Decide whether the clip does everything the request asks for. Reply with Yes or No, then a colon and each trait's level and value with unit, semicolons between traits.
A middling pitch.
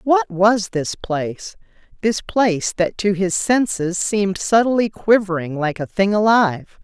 No: high, 195 Hz